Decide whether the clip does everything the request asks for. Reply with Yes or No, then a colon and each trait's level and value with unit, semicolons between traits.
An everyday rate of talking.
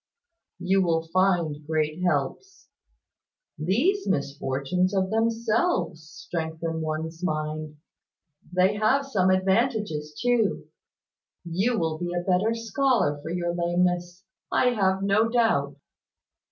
No: slow, 110 wpm